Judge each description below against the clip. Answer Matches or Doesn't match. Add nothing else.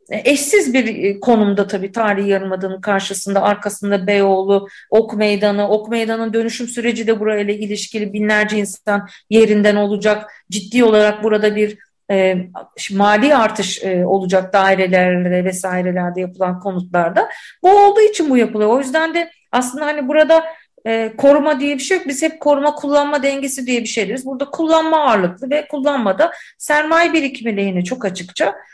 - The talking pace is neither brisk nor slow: Doesn't match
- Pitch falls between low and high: Doesn't match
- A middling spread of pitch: Doesn't match